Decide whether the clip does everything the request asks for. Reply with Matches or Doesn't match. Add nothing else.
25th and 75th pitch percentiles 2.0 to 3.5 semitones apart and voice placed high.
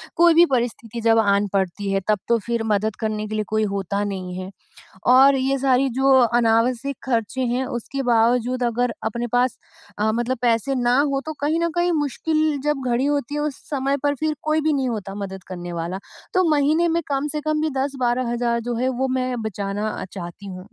Doesn't match